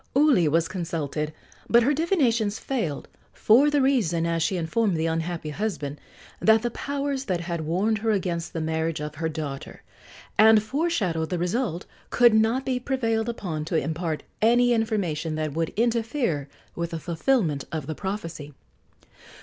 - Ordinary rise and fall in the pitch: No, wide, 6.4 semitones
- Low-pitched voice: No, medium, 180 Hz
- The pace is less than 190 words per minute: Yes, average, 160 wpm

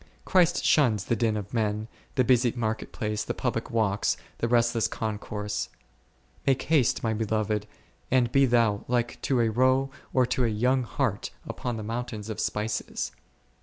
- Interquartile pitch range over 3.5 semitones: No, average, 2.7 semitones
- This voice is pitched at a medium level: No, low, 115 Hz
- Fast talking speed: No, average, 165 wpm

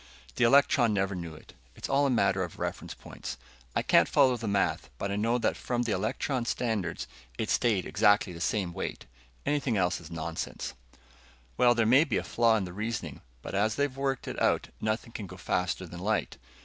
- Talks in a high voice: No, low, 110 Hz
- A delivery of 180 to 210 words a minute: Yes, average, 200 wpm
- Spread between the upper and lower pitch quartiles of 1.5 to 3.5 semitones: No, average, 4.5 semitones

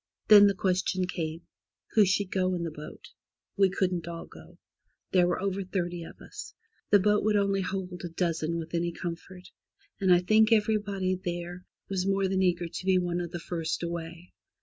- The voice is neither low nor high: Yes, medium, 180 Hz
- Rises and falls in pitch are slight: Yes, narrow, 2.2 semitones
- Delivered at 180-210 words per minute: Yes, average, 190 wpm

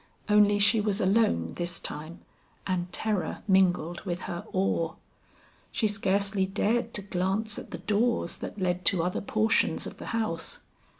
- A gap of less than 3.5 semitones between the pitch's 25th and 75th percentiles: Yes, average, 3.0 semitones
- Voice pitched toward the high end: Yes, high, 195 Hz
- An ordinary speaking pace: Yes, average, 155 wpm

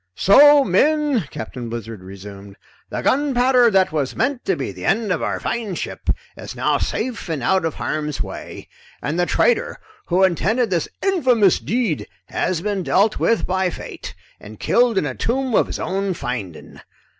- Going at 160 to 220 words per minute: Yes, average, 170 wpm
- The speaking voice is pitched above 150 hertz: Yes, high, 190 Hz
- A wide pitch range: Yes, wide, 8.5 semitones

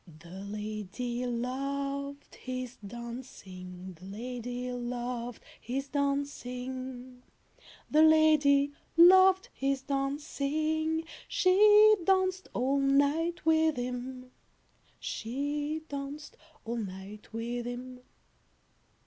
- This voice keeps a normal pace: No, slow, 85 wpm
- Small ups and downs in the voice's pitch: No, average, 3.4 semitones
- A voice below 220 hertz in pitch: No, very high, 260 Hz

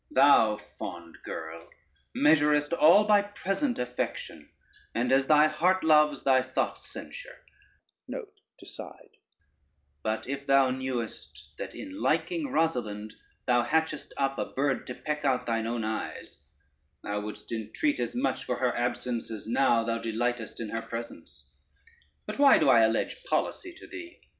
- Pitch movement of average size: No, wide, 5.9 semitones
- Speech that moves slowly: No, average, 145 wpm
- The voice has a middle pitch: No, low, 130 Hz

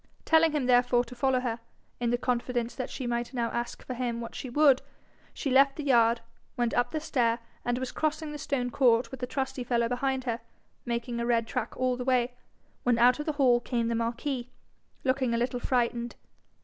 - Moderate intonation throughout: No, narrow, 1.9 semitones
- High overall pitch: Yes, high, 245 Hz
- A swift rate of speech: Yes, fast, 210 wpm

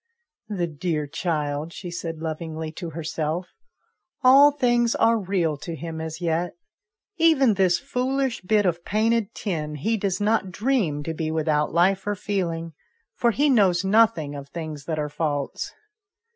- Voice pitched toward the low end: No, medium, 175 Hz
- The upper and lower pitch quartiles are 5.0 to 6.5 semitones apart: Yes, wide, 5.5 semitones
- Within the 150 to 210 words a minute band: Yes, average, 165 wpm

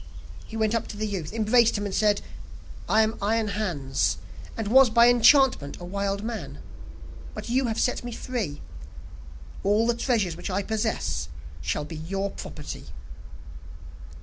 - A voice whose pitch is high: Yes, high, 215 Hz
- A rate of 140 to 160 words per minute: Yes, average, 155 wpm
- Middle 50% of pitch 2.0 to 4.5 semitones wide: Yes, average, 3.0 semitones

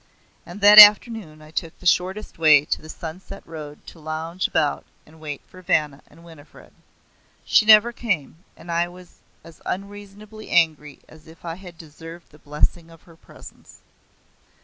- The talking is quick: No, average, 170 wpm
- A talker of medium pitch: Yes, medium, 165 Hz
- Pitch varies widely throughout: No, average, 3.5 semitones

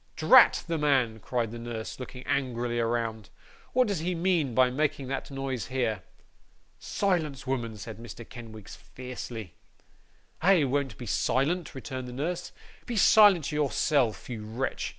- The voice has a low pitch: Yes, low, 130 Hz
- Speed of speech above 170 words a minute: No, average, 145 wpm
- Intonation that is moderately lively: Yes, average, 4.4 semitones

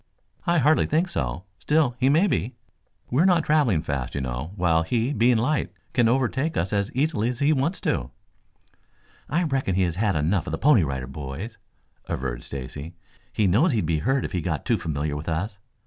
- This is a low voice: Yes, low, 105 Hz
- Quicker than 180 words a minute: Yes, average, 195 wpm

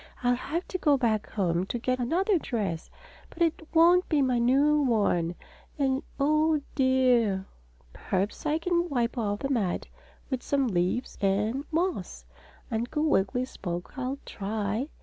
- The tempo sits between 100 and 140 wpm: No, average, 150 wpm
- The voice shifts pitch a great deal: Yes, wide, 6.4 semitones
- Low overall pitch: No, very high, 255 Hz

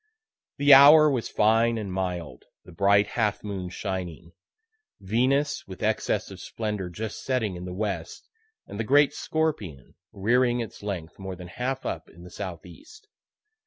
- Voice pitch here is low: Yes, low, 105 Hz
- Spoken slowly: No, average, 155 wpm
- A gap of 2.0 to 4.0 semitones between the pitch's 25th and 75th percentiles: No, average, 5.2 semitones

